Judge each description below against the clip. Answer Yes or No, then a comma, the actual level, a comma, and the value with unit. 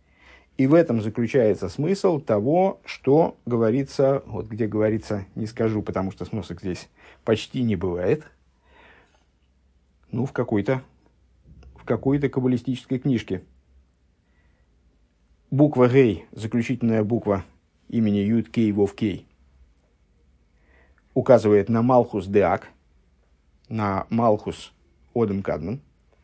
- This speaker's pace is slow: Yes, slow, 105 wpm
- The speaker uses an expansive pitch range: Yes, wide, 8.4 semitones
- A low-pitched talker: Yes, low, 100 Hz